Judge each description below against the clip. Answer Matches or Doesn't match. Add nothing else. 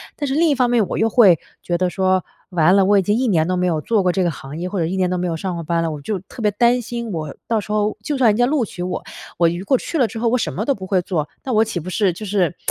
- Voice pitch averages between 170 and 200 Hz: Matches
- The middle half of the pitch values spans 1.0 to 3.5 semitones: Doesn't match